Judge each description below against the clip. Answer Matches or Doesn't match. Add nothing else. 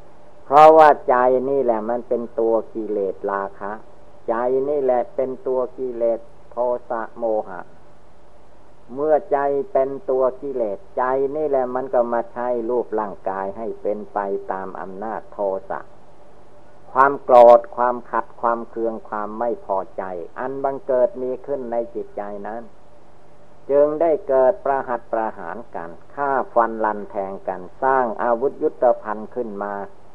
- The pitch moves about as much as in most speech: Matches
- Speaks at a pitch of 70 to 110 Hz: Doesn't match